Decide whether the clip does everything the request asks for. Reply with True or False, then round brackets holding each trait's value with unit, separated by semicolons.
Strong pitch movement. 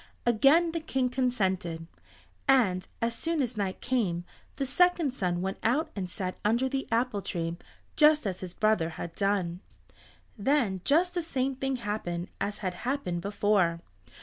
True (6.6 semitones)